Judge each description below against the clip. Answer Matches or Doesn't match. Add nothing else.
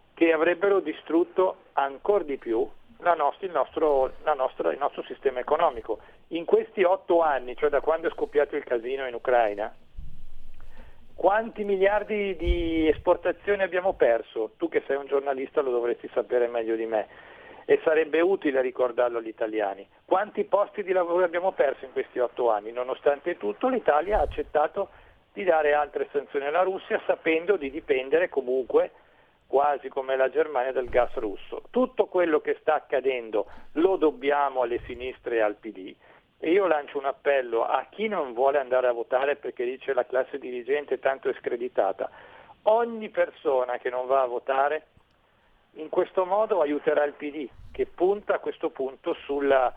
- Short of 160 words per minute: Doesn't match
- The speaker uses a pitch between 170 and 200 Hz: Matches